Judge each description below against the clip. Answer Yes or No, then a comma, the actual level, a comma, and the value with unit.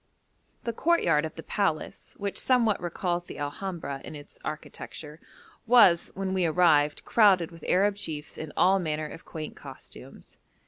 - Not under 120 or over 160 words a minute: Yes, average, 150 wpm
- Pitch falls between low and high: Yes, medium, 175 Hz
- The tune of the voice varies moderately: Yes, average, 4.2 semitones